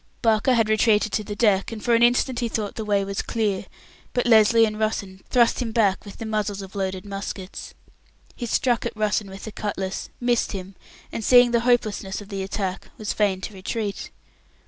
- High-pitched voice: Yes, high, 215 Hz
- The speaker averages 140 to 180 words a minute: No, fast, 205 wpm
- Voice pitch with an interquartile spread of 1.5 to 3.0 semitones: Yes, narrow, 2.6 semitones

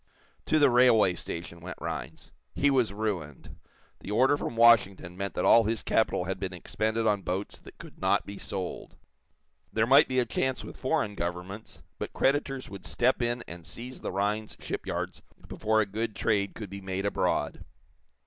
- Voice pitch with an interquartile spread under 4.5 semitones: Yes, average, 3.8 semitones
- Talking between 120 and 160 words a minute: No, average, 175 wpm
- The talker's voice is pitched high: No, low, 105 Hz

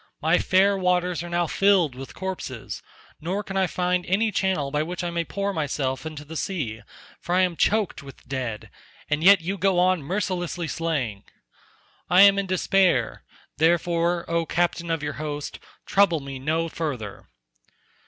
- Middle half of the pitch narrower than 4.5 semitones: Yes, average, 3.9 semitones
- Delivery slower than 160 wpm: No, average, 165 wpm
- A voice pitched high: No, medium, 170 Hz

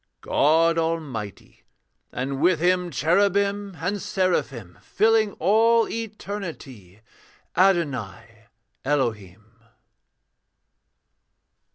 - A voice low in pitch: No, medium, 165 Hz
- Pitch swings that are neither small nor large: No, wide, 8.8 semitones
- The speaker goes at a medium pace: No, slow, 65 wpm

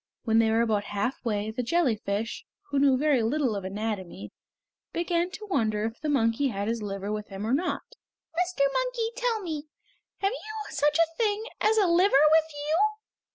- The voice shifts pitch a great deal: Yes, wide, 7.9 semitones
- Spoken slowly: No, average, 180 wpm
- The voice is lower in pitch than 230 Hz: No, very high, 275 Hz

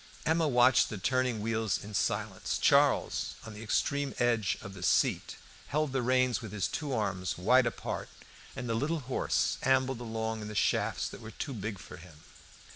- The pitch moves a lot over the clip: No, average, 3.7 semitones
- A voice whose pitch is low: Yes, low, 115 Hz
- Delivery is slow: No, average, 185 wpm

